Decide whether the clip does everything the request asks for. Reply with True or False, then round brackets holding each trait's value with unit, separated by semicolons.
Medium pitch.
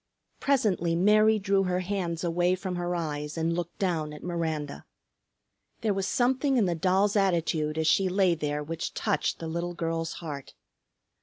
True (175 Hz)